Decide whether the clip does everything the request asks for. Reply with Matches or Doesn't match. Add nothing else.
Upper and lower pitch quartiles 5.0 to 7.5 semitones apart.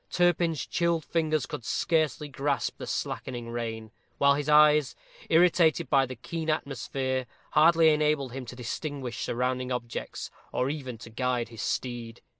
Doesn't match